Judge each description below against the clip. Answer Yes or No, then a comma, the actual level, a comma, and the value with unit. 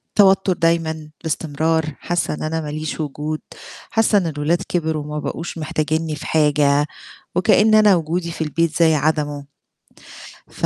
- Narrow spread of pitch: Yes, narrow, 1.9 semitones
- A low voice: No, medium, 160 Hz